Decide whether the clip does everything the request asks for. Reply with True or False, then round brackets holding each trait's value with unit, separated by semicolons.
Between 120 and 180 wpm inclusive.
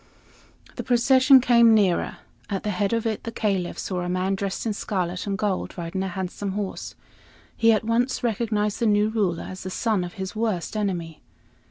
False (190 wpm)